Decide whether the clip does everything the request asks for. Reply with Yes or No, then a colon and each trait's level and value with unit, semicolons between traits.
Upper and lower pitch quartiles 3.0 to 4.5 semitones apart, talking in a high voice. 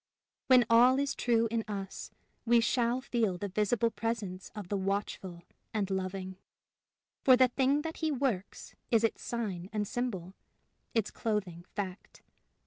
Yes: average, 4.1 semitones; high, 220 Hz